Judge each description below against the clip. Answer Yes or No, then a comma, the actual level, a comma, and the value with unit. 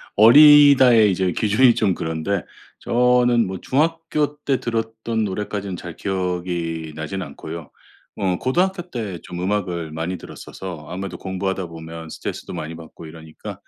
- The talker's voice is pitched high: No, very low, 95 Hz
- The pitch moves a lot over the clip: Yes, wide, 5.9 semitones